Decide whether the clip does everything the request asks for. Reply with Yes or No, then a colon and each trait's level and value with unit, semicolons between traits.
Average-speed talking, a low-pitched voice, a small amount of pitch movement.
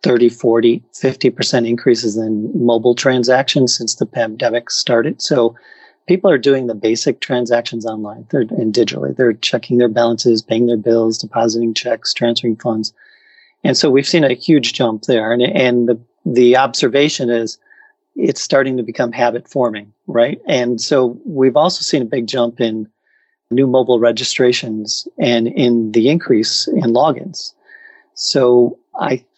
Yes: average, 150 wpm; low, 120 Hz; narrow, 2.3 semitones